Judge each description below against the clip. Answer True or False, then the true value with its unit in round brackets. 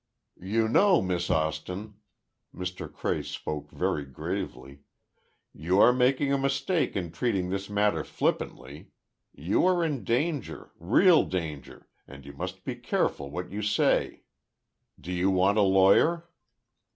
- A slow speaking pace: True (130 wpm)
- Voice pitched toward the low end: True (95 Hz)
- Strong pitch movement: True (6.3 semitones)